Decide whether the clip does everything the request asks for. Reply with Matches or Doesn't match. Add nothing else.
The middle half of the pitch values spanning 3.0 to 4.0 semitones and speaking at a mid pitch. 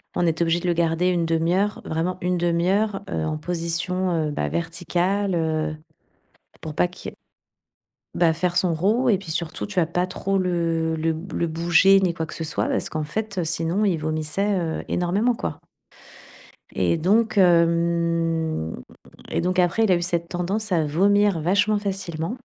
Doesn't match